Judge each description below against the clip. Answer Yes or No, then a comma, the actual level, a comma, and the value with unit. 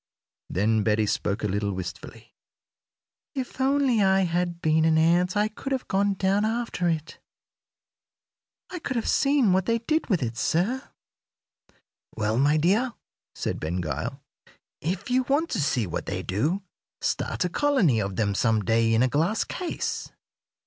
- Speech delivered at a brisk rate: No, average, 160 wpm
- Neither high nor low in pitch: Yes, medium, 175 Hz